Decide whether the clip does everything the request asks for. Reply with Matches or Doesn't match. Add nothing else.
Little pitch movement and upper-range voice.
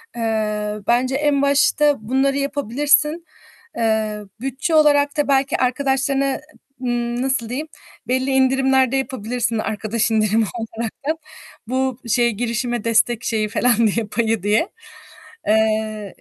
Doesn't match